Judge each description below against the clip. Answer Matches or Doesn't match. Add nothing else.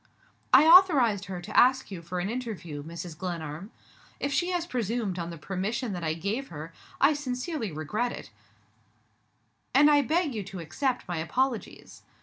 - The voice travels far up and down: Matches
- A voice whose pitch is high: Matches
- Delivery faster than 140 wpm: Matches